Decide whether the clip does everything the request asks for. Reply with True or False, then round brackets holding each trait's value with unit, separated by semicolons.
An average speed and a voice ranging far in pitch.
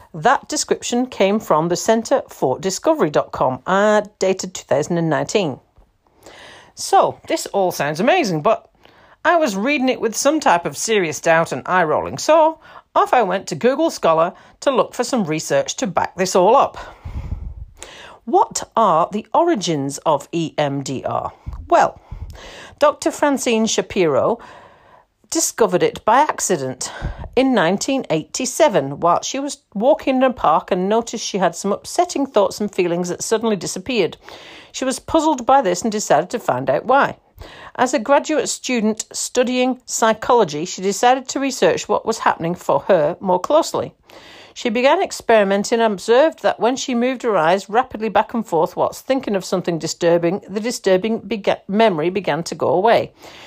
True (155 wpm; 6.1 semitones)